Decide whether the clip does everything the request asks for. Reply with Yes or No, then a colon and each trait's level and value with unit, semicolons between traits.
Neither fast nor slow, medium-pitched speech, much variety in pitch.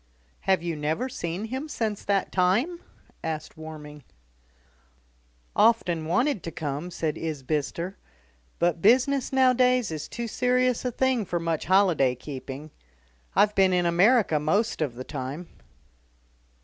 No: slow, 130 wpm; medium, 180 Hz; wide, 7.1 semitones